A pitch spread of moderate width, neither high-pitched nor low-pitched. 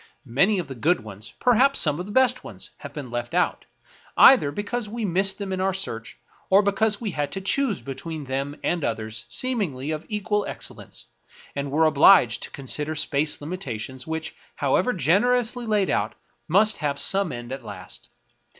No: wide, 7.1 semitones; medium, 160 Hz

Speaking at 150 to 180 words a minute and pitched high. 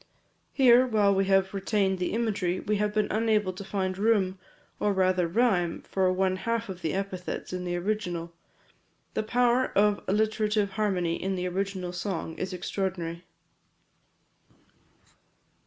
No: average, 140 wpm; high, 195 Hz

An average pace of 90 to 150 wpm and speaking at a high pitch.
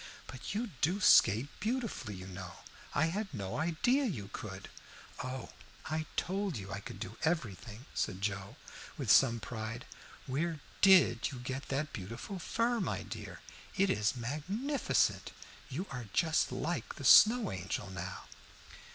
No: average, 145 wpm; low, 135 Hz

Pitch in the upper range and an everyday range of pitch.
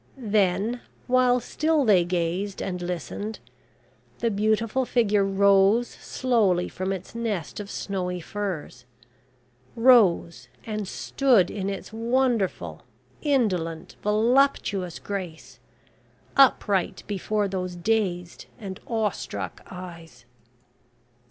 Yes: high, 200 Hz; average, 4.1 semitones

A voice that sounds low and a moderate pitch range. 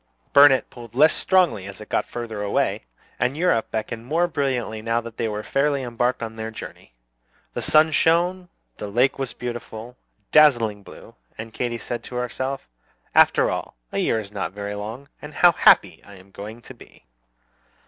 Yes: low, 120 Hz; average, 4.2 semitones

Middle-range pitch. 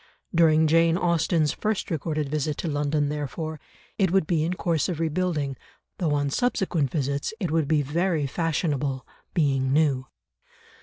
Yes: medium, 155 Hz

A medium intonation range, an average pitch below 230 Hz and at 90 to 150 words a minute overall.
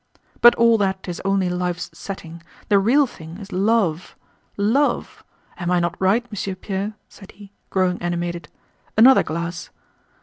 Yes: average, 3.3 semitones; high, 190 Hz; average, 140 wpm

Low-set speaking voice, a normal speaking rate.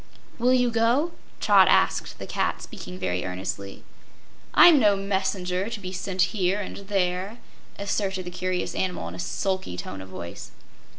No: high, 190 Hz; average, 160 wpm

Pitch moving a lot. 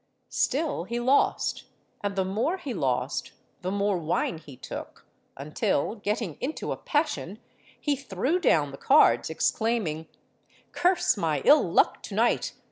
Yes: wide, 8.7 semitones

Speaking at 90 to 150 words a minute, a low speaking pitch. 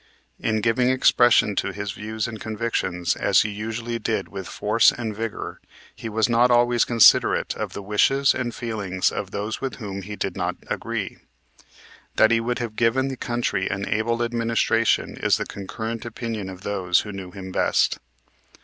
No: average, 175 wpm; low, 110 Hz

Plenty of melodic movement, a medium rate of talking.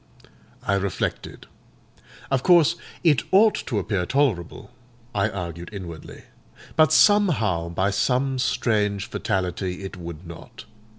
No: wide, 7.1 semitones; slow, 115 wpm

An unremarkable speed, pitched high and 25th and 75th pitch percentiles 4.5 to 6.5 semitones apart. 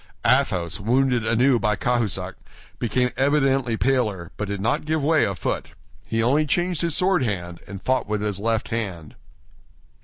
No: average, 160 wpm; low, 115 Hz; average, 4.9 semitones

